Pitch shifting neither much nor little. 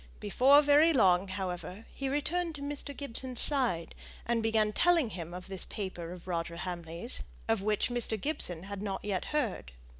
No: wide, 7.4 semitones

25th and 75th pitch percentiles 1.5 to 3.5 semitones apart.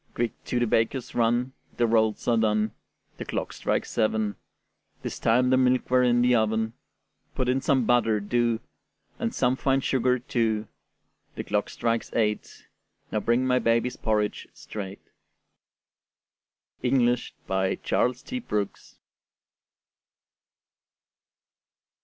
Yes: narrow, 2.4 semitones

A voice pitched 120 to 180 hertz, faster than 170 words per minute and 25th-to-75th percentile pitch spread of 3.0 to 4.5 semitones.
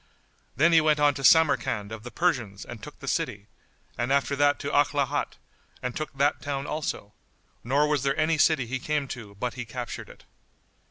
Yes: medium, 140 Hz; average, 195 wpm; average, 3.5 semitones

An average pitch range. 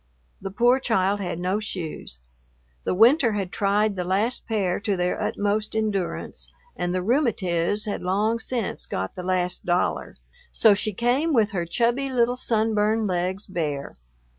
Yes: average, 3.7 semitones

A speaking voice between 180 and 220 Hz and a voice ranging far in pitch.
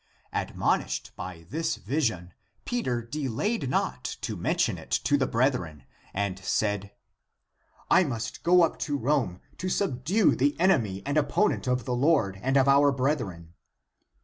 No: low, 130 Hz; wide, 6.6 semitones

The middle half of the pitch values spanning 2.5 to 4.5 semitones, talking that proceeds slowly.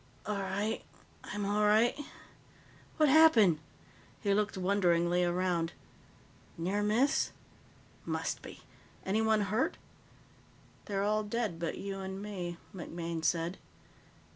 Yes: average, 3.2 semitones; slow, 110 wpm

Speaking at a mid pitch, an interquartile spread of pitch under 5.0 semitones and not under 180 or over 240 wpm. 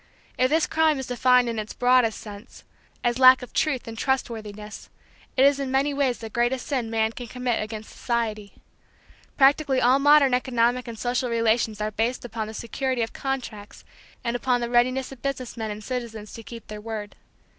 No: high, 240 Hz; average, 2.7 semitones; average, 190 wpm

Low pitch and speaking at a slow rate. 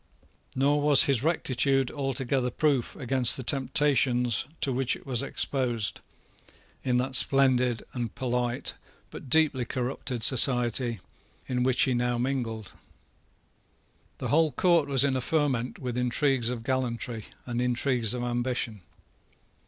Yes: low, 125 Hz; slow, 130 wpm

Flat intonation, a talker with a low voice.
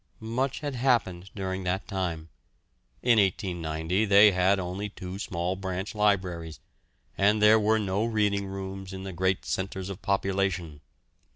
Yes: narrow, 2.2 semitones; very low, 95 Hz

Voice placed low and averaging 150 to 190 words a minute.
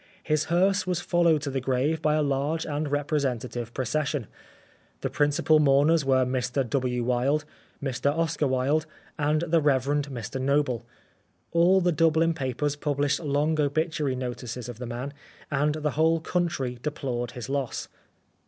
No: medium, 145 Hz; average, 155 wpm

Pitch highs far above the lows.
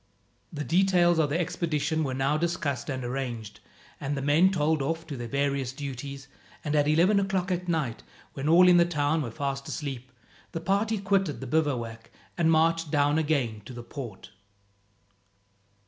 No: average, 3.8 semitones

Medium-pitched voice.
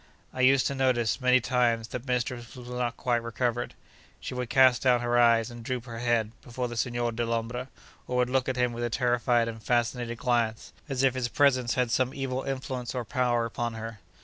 No: low, 120 Hz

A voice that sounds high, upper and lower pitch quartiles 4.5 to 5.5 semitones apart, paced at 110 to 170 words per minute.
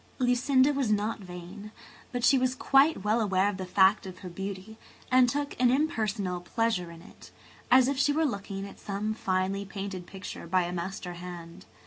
No: high, 200 Hz; average, 4.9 semitones; average, 185 wpm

